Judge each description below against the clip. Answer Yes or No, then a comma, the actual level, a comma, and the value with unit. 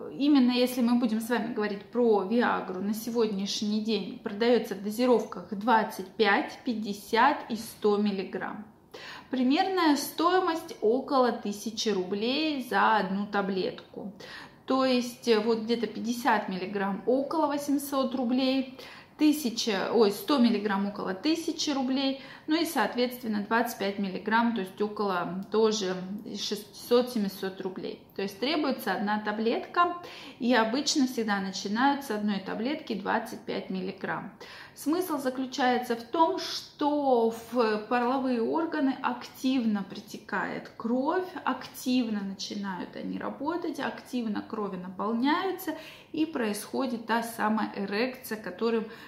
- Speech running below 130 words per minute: Yes, average, 115 wpm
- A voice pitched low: No, high, 230 Hz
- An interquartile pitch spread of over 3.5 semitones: Yes, average, 4.0 semitones